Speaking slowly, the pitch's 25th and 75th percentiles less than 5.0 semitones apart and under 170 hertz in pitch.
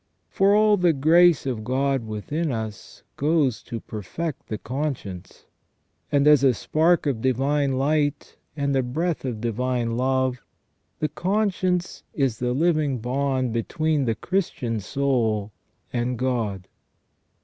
Yes: slow, 130 wpm; average, 4.6 semitones; low, 135 Hz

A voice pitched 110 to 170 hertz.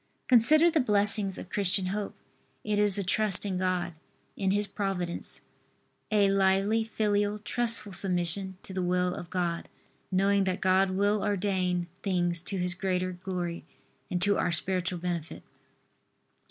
No: high, 190 Hz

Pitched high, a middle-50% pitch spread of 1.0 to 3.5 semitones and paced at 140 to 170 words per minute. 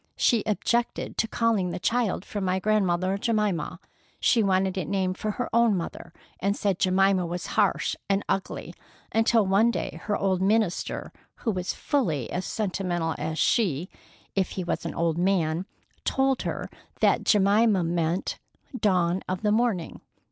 Yes: high, 195 Hz; average, 3.1 semitones; average, 155 wpm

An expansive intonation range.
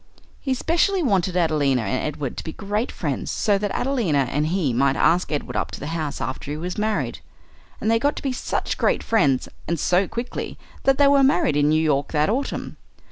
Yes: wide, 7.7 semitones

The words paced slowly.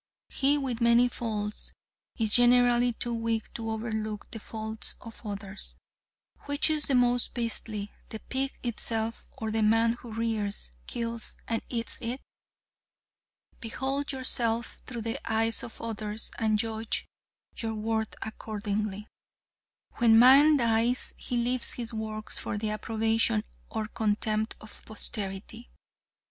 Yes: slow, 130 wpm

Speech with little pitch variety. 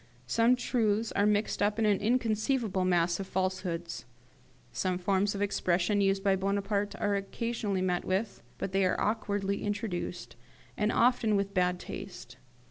Yes: narrow, 2.2 semitones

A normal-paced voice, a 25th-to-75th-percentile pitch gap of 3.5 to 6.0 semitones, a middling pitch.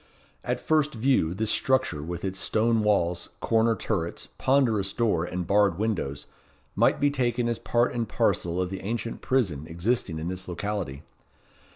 No: average, 160 wpm; average, 5.2 semitones; low, 105 Hz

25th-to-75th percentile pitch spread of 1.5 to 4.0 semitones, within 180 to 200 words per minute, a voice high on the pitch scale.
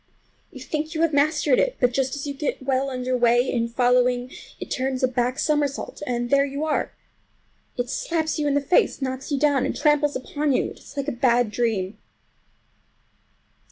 Yes: average, 2.9 semitones; average, 195 wpm; very high, 265 Hz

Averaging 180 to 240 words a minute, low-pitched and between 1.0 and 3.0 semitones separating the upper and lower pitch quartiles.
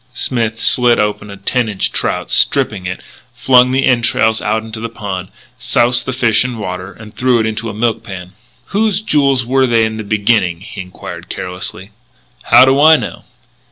No: average, 185 wpm; low, 110 Hz; average, 3.5 semitones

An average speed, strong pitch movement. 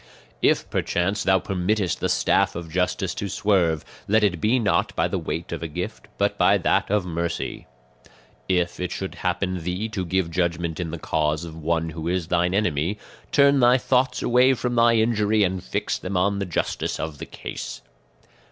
No: average, 190 wpm; average, 3.8 semitones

